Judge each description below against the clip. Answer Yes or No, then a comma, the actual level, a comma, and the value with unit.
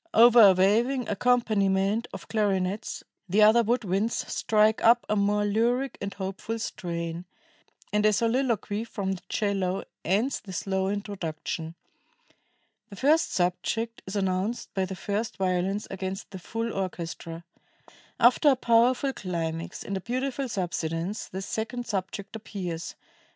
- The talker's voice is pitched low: No, high, 205 Hz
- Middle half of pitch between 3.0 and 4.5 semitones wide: Yes, average, 3.4 semitones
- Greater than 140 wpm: No, slow, 135 wpm